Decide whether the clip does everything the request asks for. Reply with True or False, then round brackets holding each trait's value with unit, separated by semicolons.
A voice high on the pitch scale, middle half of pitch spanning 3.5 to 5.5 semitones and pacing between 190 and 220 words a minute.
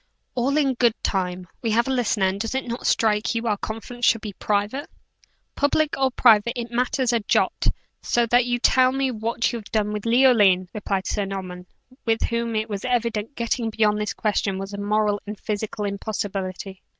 False (220 Hz; 2.9 semitones; 195 wpm)